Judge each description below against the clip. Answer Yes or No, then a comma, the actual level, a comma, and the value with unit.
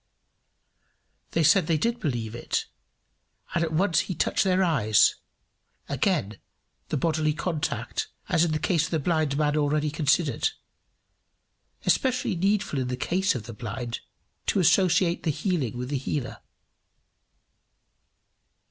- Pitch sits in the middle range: Yes, medium, 155 Hz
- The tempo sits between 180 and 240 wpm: No, slow, 135 wpm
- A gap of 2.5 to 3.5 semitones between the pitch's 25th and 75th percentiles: No, average, 4.5 semitones